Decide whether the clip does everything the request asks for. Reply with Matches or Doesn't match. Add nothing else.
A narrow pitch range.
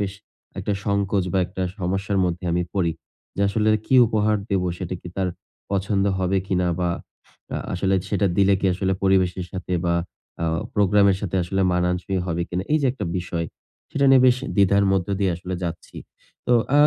Matches